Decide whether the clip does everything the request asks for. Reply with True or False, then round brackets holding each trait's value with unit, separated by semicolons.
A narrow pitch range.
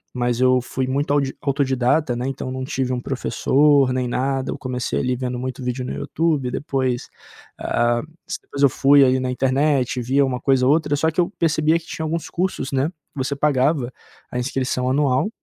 True (2.1 semitones)